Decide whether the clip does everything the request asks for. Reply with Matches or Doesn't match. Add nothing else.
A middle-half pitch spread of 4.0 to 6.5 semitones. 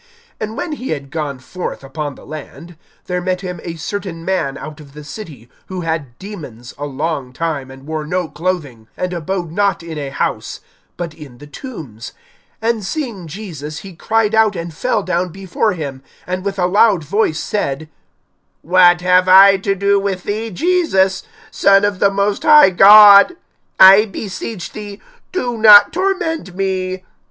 Matches